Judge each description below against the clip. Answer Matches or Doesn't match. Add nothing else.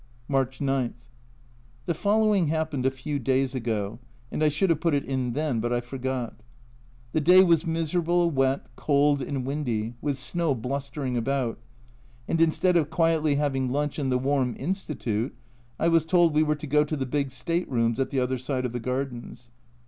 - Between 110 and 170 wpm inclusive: Doesn't match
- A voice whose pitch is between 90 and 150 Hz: Matches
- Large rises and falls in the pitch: Doesn't match